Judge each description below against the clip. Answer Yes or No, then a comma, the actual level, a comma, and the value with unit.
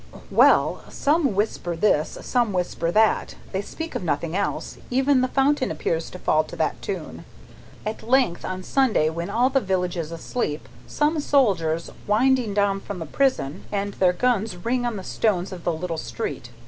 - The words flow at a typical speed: Yes, average, 180 wpm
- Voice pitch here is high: Yes, high, 200 Hz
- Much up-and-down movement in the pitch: Yes, wide, 6.4 semitones